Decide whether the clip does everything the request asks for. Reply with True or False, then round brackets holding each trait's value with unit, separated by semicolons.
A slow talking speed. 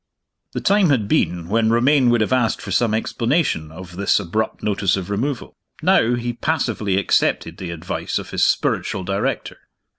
False (170 wpm)